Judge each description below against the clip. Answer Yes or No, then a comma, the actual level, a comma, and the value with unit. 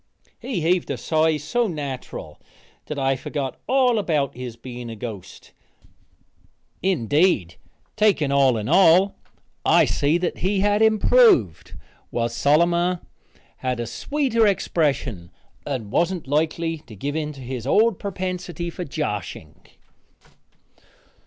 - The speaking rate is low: Yes, slow, 125 wpm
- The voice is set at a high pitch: No, medium, 155 Hz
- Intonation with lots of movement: Yes, wide, 6.4 semitones